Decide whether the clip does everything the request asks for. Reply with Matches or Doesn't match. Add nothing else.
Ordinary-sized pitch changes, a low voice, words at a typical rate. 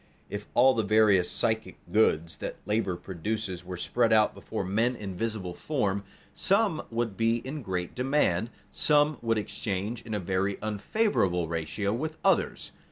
Matches